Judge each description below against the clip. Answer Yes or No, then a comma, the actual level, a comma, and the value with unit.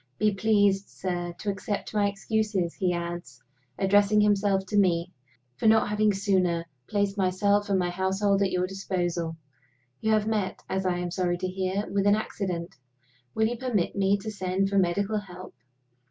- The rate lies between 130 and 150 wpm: No, average, 170 wpm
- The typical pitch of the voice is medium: No, high, 195 Hz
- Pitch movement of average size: No, narrow, 2.1 semitones